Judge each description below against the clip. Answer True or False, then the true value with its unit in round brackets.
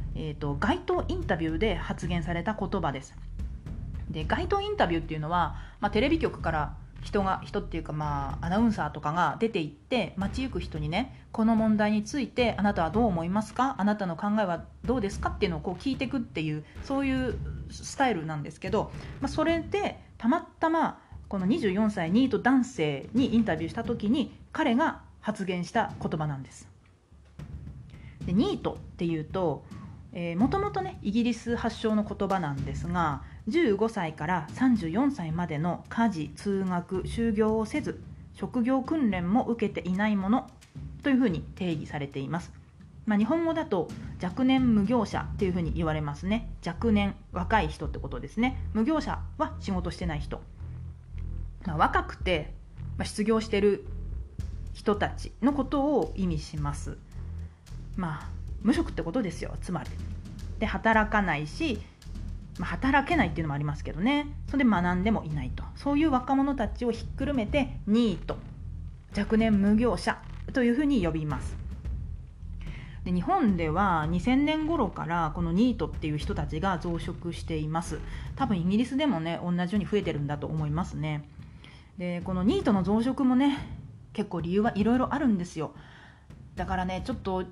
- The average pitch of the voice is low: False (195 Hz)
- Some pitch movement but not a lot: False (7.1 semitones)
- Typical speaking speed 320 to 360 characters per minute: True (325 characters per minute)